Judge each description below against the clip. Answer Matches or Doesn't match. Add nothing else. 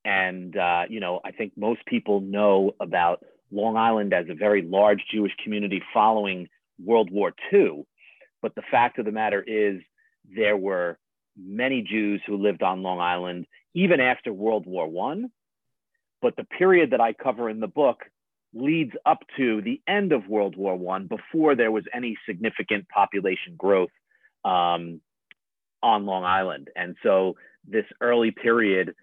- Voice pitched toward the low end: Matches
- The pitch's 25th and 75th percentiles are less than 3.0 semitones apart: Doesn't match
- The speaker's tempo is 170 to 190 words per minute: Doesn't match